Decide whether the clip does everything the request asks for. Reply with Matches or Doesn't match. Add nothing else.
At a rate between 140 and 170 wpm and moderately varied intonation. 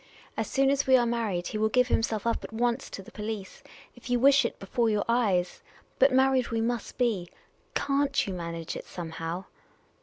Doesn't match